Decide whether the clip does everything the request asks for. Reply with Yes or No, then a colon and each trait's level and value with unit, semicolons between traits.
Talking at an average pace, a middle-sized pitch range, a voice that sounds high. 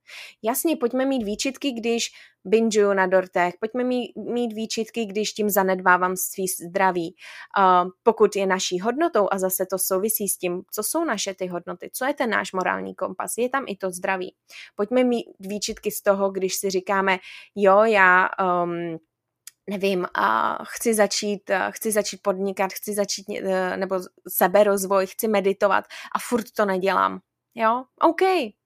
Yes: average, 155 wpm; average, 3.1 semitones; high, 200 Hz